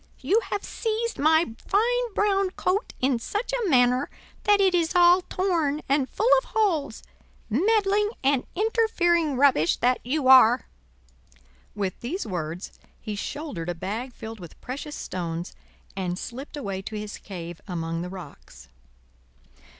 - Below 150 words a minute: Yes, average, 140 wpm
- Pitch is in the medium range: No, very high, 280 Hz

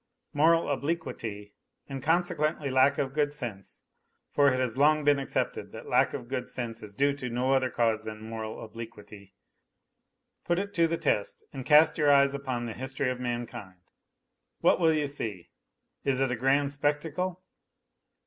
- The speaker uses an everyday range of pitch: Yes, average, 4.0 semitones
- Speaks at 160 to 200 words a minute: Yes, average, 165 wpm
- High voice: No, low, 135 Hz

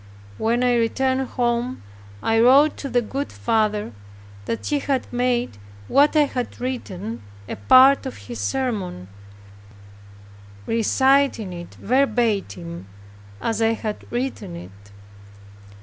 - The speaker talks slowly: Yes, slow, 120 wpm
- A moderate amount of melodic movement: Yes, average, 3.8 semitones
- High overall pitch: Yes, high, 240 Hz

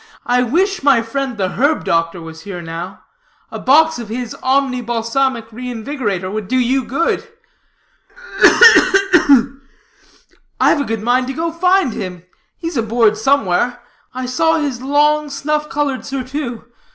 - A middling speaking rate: Yes, average, 150 wpm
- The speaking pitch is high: Yes, very high, 255 Hz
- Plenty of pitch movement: No, average, 4.2 semitones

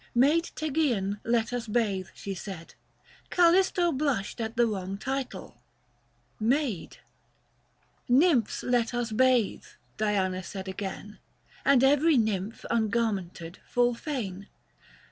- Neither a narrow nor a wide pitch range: Yes, average, 5.0 semitones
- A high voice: Yes, high, 230 Hz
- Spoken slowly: Yes, slow, 120 wpm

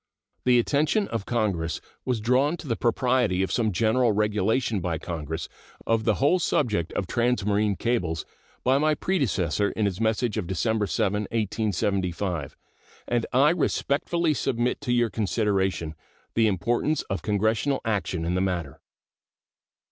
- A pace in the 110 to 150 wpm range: Yes, average, 140 wpm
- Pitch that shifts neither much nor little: Yes, average, 4.5 semitones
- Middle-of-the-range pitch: No, low, 110 Hz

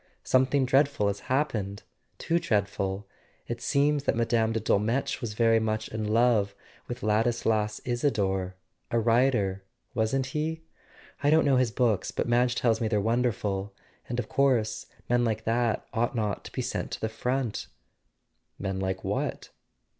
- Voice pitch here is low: Yes, low, 115 Hz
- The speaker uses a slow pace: No, average, 170 wpm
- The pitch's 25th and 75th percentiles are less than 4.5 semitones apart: Yes, average, 3.1 semitones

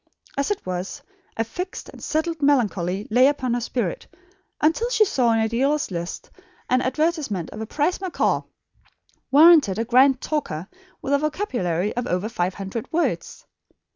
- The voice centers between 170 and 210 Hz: No, very high, 255 Hz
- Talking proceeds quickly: No, average, 160 wpm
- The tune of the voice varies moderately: No, wide, 6.6 semitones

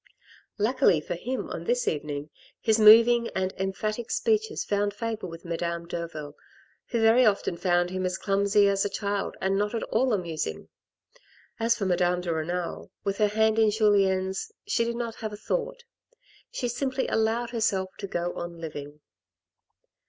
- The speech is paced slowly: No, average, 165 wpm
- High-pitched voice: Yes, high, 205 Hz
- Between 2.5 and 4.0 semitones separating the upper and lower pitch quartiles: No, average, 4.5 semitones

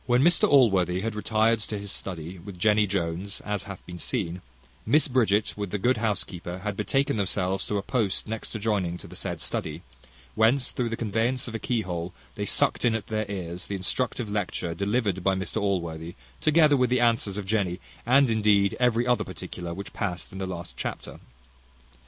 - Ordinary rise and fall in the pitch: Yes, average, 3.7 semitones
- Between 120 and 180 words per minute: No, average, 190 wpm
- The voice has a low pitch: Yes, low, 105 Hz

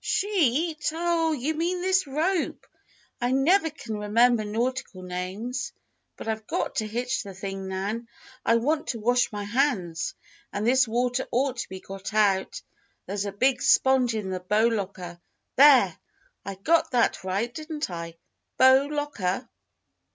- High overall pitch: Yes, high, 240 Hz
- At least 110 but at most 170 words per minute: Yes, average, 150 wpm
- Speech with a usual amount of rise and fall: No, wide, 6.1 semitones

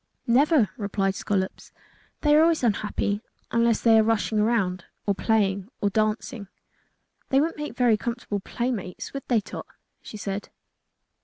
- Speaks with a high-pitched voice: Yes, high, 220 Hz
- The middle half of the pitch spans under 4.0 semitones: Yes, average, 3.1 semitones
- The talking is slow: No, average, 145 wpm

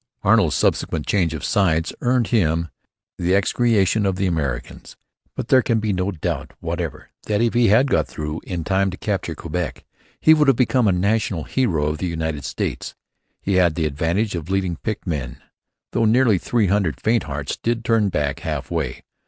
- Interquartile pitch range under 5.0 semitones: No, average, 5.3 semitones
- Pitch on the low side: Yes, very low, 95 Hz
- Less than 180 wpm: No, average, 185 wpm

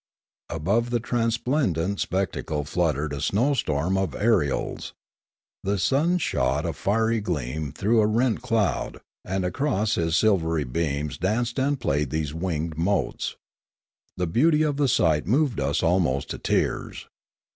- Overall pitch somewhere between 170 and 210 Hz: No, very low, 95 Hz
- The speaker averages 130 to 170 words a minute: Yes, average, 145 wpm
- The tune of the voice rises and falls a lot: Yes, wide, 6.9 semitones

